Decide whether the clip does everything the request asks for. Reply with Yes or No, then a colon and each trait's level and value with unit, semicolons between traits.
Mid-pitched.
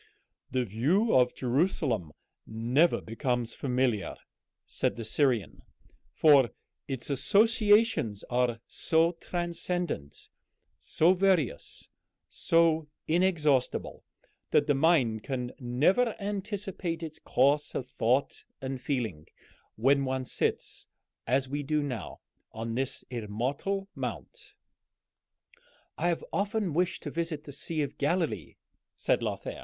Yes: medium, 145 Hz